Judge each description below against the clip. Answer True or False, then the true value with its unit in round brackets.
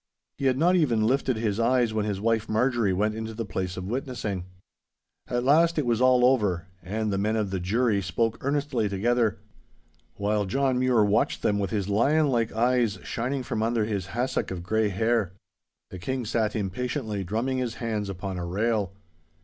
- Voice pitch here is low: True (110 Hz)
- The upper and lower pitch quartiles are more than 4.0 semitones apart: False (3.7 semitones)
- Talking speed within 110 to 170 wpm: False (180 wpm)